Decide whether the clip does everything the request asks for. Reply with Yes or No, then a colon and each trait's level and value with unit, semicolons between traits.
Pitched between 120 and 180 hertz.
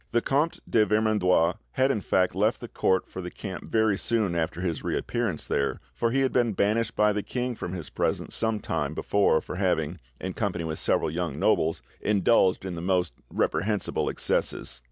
No: low, 100 Hz